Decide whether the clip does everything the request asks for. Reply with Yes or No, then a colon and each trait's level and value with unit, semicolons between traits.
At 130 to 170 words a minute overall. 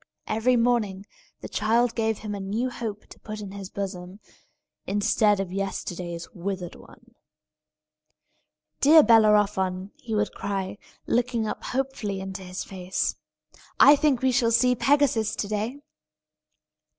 Yes: slow, 135 wpm